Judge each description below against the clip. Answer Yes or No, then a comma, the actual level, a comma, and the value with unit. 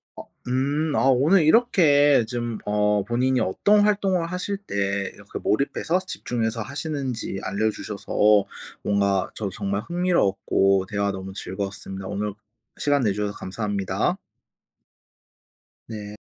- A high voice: No, low, 110 Hz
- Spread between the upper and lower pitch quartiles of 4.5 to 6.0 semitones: No, wide, 6.5 semitones